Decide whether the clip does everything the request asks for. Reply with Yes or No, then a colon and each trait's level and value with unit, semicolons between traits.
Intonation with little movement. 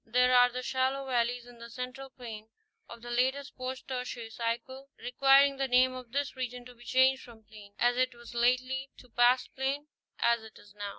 Yes: narrow, 1.7 semitones